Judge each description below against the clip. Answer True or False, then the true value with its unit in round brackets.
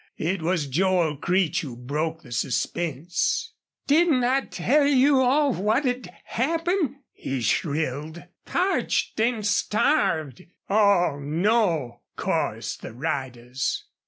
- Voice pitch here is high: False (180 Hz)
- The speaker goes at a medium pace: False (105 wpm)